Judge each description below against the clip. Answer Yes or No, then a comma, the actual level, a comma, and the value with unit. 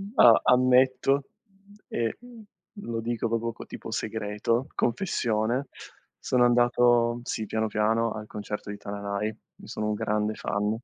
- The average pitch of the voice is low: Yes, low, 115 Hz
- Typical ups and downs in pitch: No, narrow, 2.2 semitones